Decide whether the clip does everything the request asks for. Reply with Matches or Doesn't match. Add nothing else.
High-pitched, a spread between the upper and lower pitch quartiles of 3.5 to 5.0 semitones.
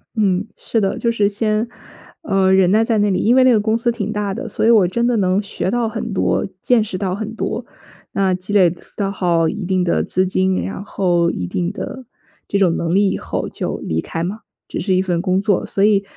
Doesn't match